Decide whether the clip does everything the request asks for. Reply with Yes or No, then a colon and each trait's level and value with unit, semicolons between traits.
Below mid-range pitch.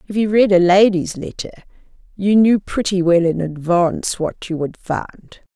No: medium, 185 Hz